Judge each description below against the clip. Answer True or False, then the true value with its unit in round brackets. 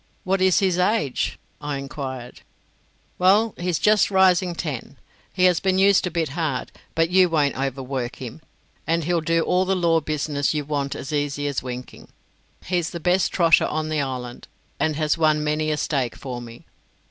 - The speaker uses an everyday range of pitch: True (4.3 semitones)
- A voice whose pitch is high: False (155 Hz)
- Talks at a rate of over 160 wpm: True (180 wpm)